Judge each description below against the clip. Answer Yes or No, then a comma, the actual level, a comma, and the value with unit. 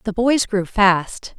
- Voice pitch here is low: No, high, 205 Hz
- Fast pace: No, average, 175 wpm